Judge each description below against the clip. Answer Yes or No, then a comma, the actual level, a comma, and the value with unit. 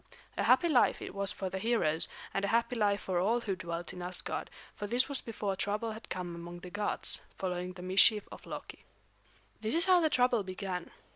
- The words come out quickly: Yes, fast, 210 wpm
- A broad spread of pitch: No, average, 4.0 semitones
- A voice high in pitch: Yes, high, 200 Hz